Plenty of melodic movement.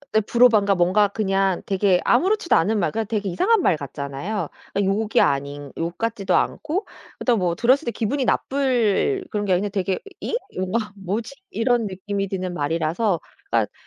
No: average, 4.1 semitones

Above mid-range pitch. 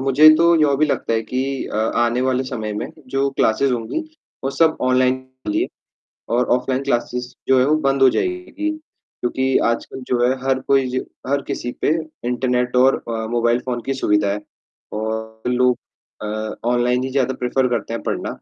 No: low, 125 Hz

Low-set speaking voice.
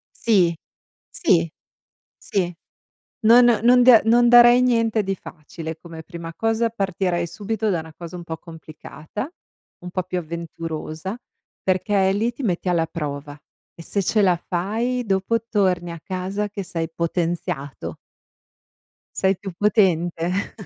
No: medium, 185 Hz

